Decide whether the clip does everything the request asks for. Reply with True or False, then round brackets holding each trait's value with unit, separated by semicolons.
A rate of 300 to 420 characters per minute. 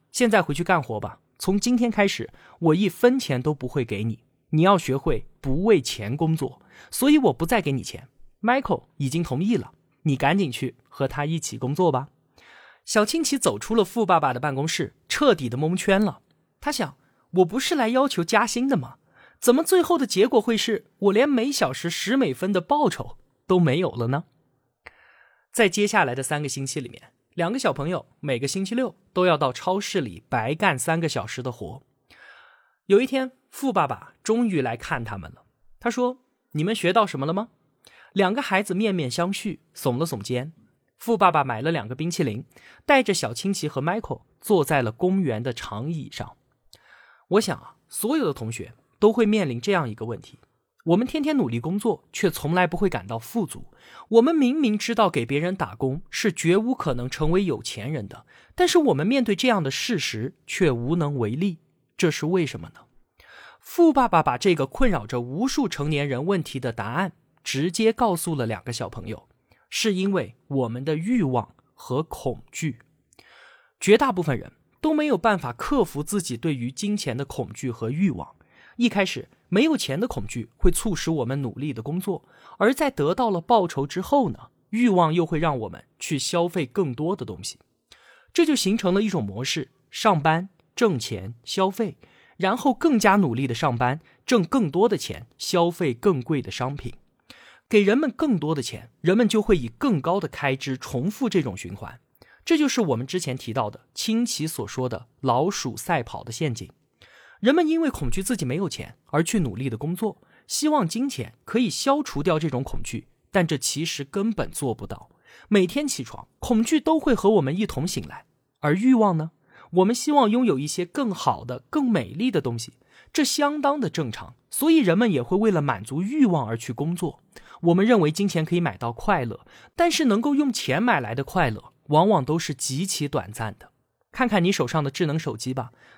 False (275 characters per minute)